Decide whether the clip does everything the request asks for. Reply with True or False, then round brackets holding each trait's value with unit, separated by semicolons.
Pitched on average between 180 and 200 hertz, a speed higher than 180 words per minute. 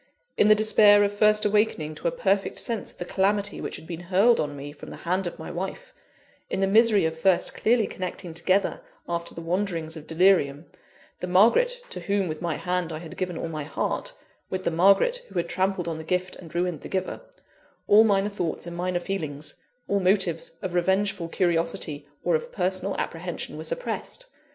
True (185 Hz; 200 wpm)